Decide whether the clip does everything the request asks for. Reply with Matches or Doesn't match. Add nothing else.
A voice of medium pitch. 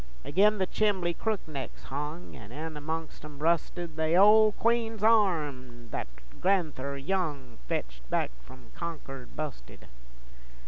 Matches